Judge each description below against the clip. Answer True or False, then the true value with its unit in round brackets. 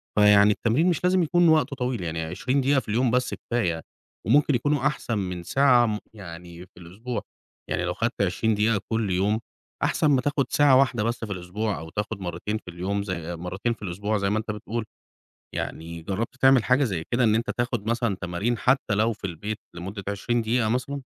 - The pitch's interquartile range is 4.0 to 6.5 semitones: True (4.7 semitones)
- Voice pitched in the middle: False (110 Hz)